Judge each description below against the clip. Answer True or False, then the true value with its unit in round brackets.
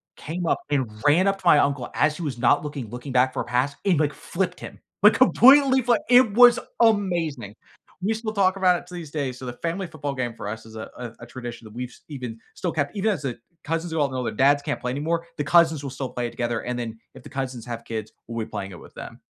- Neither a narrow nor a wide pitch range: False (6.3 semitones)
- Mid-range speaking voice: True (145 Hz)